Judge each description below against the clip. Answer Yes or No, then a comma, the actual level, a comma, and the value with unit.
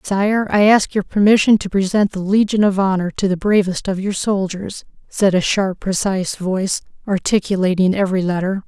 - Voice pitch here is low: No, high, 195 Hz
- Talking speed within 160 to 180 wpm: Yes, average, 175 wpm